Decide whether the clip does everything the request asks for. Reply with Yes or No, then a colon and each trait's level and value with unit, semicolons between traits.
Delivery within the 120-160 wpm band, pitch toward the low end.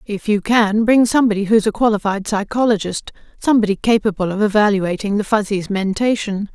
No: average, 145 wpm; high, 210 Hz